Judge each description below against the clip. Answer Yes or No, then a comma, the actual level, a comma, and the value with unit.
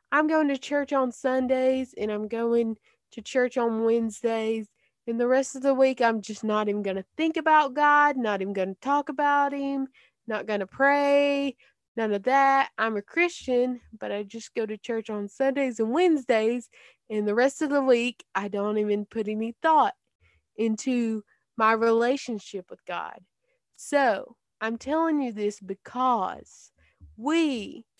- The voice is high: Yes, high, 240 Hz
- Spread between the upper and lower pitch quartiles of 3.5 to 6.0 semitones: Yes, average, 4.2 semitones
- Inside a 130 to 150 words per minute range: No, average, 170 wpm